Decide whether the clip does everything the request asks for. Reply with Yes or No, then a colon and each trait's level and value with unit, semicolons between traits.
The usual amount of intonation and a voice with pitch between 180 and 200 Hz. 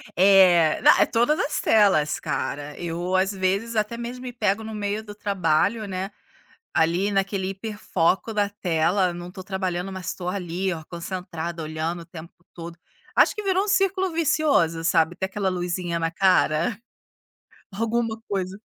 Yes: average, 3.7 semitones; high, 190 Hz